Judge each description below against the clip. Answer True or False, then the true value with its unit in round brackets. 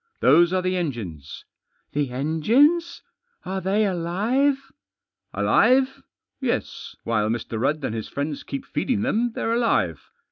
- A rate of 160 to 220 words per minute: False (150 wpm)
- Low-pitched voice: False (185 Hz)